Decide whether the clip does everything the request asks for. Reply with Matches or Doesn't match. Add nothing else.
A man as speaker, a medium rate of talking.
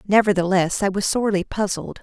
Doesn't match